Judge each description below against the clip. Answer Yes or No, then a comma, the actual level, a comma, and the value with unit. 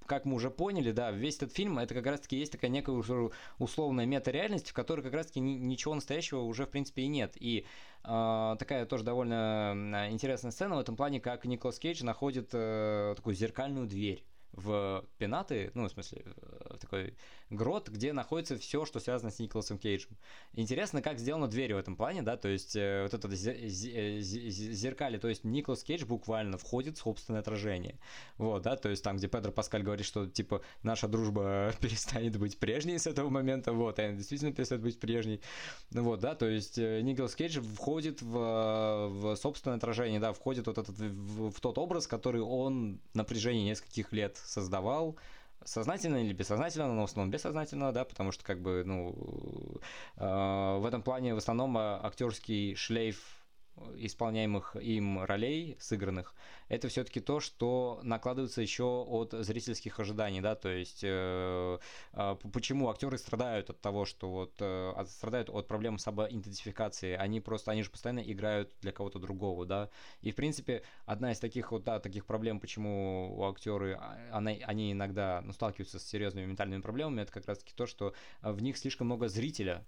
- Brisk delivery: Yes, fast, 170 wpm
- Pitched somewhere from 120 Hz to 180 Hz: No, low, 110 Hz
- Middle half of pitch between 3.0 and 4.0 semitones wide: Yes, average, 3.7 semitones